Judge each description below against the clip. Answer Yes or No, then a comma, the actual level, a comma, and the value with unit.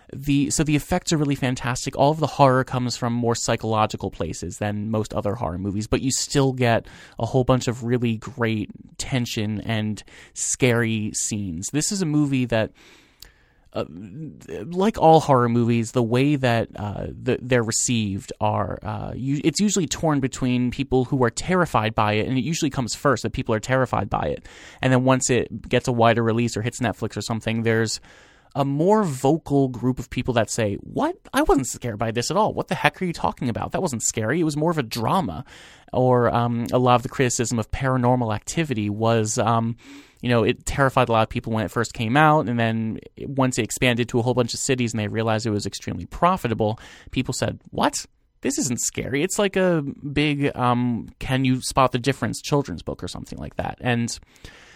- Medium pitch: No, low, 125 Hz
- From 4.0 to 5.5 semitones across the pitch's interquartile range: No, average, 3.4 semitones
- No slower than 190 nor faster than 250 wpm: Yes, fast, 205 wpm